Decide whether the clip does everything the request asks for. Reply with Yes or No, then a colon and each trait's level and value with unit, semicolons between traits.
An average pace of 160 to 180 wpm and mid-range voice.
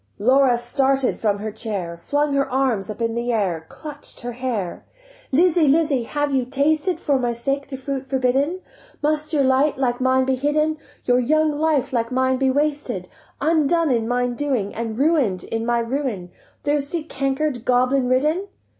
No: average, 170 wpm; very high, 265 Hz